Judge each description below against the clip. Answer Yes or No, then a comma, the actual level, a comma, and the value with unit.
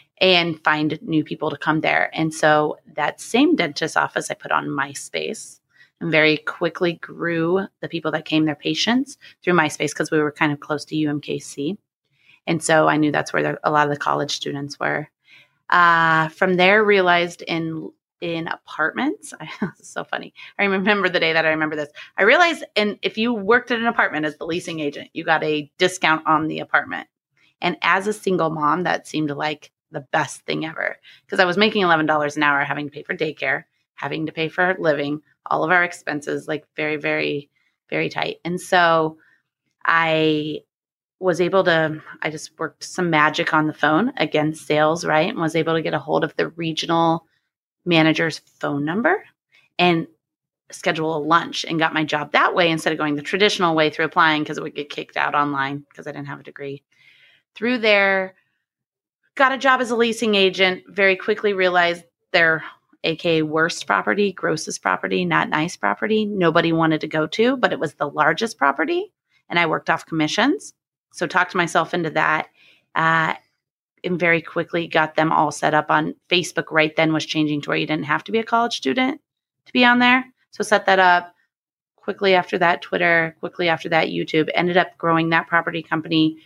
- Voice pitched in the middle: Yes, medium, 165 Hz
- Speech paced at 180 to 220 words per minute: Yes, average, 190 wpm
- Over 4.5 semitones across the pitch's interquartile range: No, average, 3.0 semitones